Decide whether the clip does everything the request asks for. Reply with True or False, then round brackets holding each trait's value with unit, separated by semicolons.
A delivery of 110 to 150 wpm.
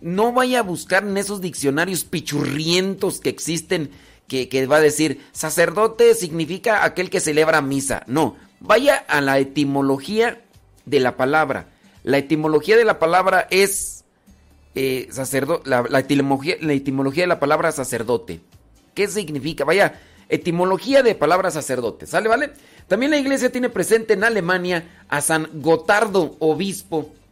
True (145 wpm)